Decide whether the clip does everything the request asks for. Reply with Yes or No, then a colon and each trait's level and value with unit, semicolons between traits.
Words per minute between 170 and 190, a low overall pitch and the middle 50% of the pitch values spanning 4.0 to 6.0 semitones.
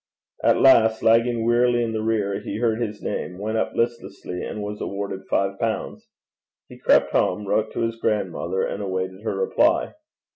No: average, 175 wpm; low, 110 Hz; average, 2.8 semitones